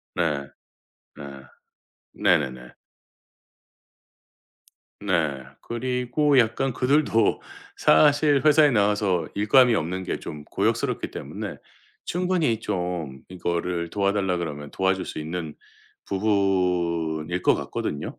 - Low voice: Yes, very low, 95 Hz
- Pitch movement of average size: No, wide, 6.2 semitones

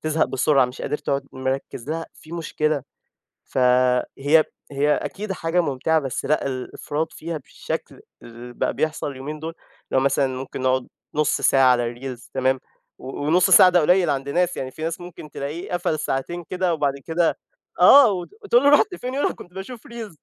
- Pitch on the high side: No, medium, 150 Hz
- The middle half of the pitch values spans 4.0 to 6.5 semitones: Yes, average, 4.7 semitones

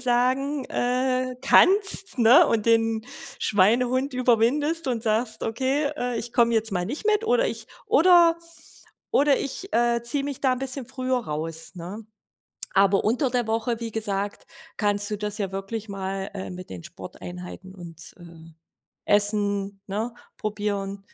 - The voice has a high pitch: Yes, high, 225 Hz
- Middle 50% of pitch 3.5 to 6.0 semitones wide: Yes, average, 4.4 semitones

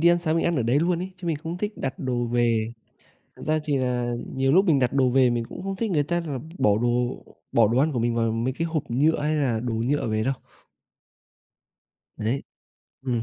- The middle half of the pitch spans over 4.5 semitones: Yes, average, 5.1 semitones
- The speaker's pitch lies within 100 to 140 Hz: Yes, low, 135 Hz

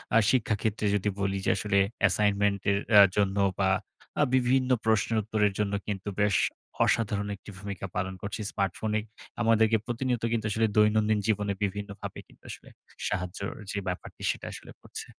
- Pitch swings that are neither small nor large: No, narrow, 1.8 semitones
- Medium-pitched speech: No, low, 105 Hz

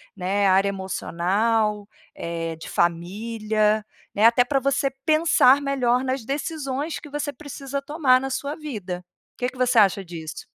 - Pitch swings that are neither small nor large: No, wide, 5.9 semitones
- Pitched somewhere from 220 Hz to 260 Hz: Yes, high, 230 Hz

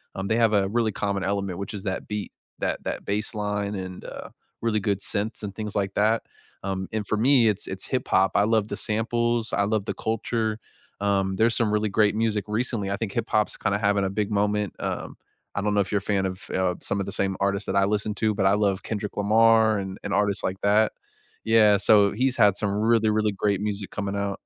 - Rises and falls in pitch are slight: Yes, narrow, 1.6 semitones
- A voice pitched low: Yes, low, 105 Hz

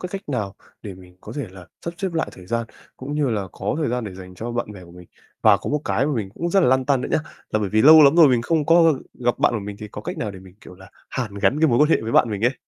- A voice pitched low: Yes, low, 120 Hz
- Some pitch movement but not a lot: No, wide, 6.9 semitones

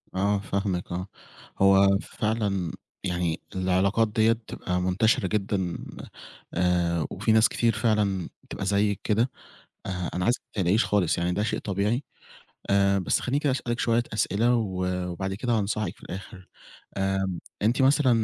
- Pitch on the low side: Yes, low, 100 Hz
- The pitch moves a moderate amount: Yes, average, 3.2 semitones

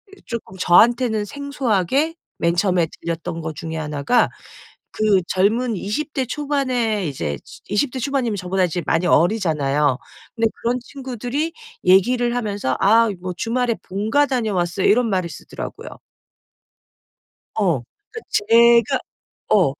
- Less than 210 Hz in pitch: No, high, 215 Hz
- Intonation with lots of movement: Yes, wide, 5.8 semitones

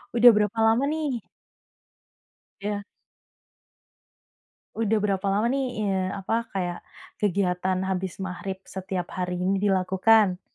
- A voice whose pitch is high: Yes, high, 195 Hz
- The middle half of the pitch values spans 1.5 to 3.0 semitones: Yes, average, 2.7 semitones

